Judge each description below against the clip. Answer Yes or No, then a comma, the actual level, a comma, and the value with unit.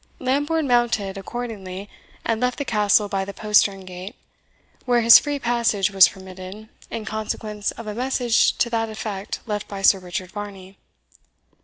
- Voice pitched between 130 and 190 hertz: No, high, 210 Hz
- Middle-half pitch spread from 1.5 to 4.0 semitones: Yes, average, 3.4 semitones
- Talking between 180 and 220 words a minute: No, average, 155 wpm